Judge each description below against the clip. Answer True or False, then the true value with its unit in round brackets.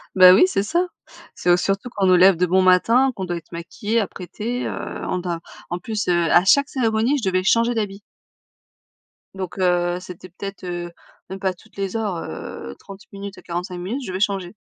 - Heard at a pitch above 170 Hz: True (190 Hz)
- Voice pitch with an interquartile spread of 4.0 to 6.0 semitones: False (3.1 semitones)